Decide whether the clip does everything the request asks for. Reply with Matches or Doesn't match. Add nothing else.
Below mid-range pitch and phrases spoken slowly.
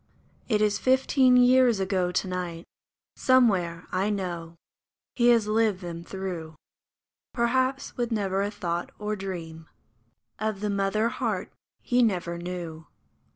Doesn't match